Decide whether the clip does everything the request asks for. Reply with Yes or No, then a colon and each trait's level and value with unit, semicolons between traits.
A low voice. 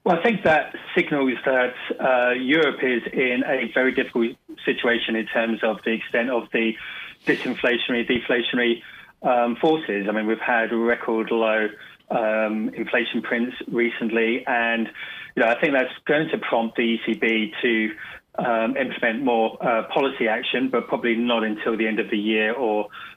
Yes: low, 115 Hz